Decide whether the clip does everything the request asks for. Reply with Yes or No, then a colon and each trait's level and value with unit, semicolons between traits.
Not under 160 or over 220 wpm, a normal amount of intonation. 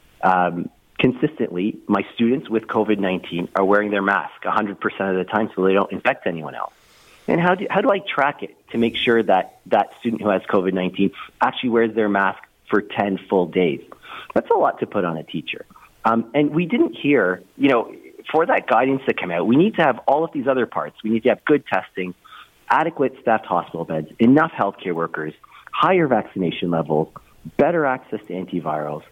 Yes: fast, 205 wpm; average, 4.2 semitones